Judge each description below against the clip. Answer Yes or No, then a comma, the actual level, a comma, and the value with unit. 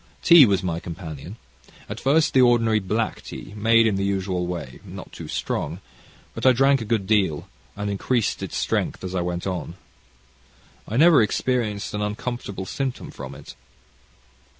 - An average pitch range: Yes, average, 4.6 semitones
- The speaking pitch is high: No, low, 105 Hz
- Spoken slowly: No, average, 165 wpm